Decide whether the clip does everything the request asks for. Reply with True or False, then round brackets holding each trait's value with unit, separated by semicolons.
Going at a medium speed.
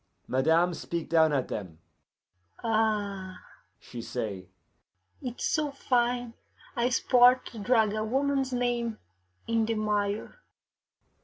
False (115 wpm)